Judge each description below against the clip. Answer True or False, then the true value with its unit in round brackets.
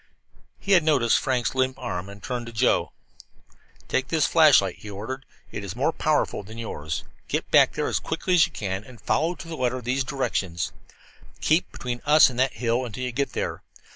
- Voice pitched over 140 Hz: False (125 Hz)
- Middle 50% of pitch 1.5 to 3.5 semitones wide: False (4.5 semitones)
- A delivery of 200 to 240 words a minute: True (205 wpm)